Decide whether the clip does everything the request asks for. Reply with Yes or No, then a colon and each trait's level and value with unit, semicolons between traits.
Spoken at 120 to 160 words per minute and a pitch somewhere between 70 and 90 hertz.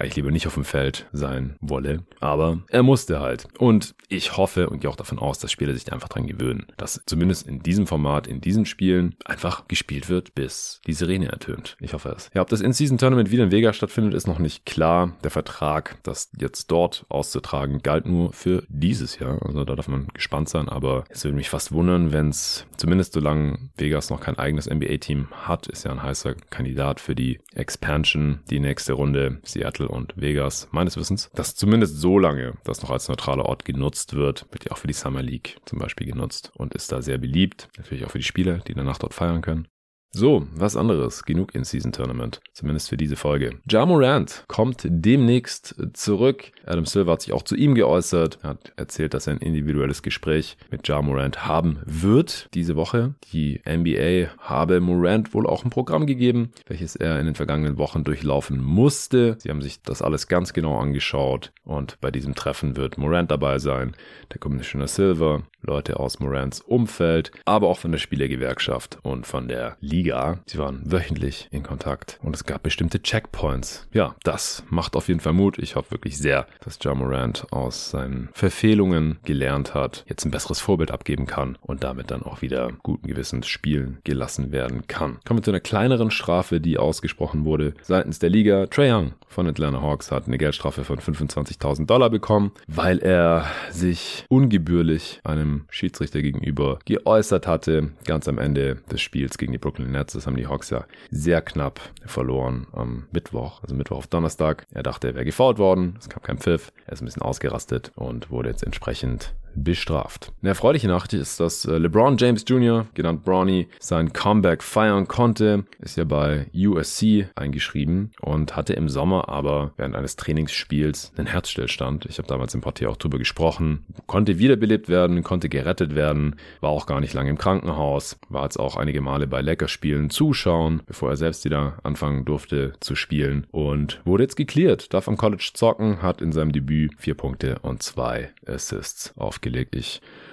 No: fast, 190 wpm; very low, 75 Hz